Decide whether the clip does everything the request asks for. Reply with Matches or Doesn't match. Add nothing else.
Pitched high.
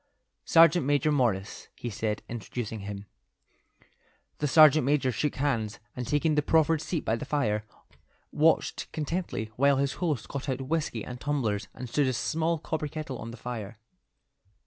Doesn't match